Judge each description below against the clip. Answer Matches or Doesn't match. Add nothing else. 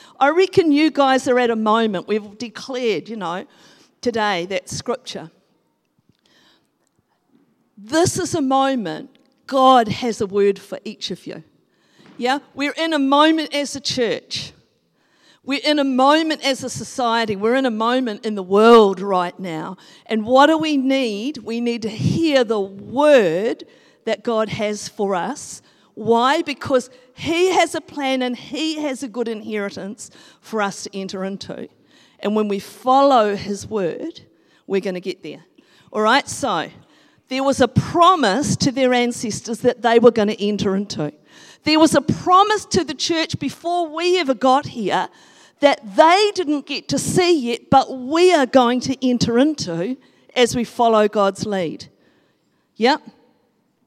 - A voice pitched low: Doesn't match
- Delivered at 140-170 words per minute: Matches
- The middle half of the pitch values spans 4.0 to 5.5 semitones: Matches